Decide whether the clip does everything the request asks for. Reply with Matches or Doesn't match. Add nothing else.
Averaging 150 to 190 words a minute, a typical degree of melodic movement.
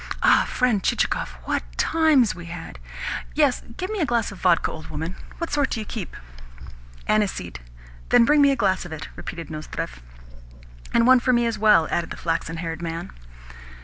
Doesn't match